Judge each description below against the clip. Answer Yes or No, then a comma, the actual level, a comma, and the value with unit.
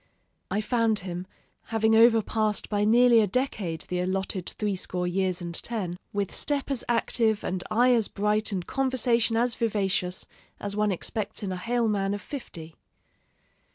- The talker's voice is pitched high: Yes, high, 210 Hz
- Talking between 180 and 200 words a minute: No, average, 155 wpm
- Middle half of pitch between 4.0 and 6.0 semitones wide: No, average, 3.6 semitones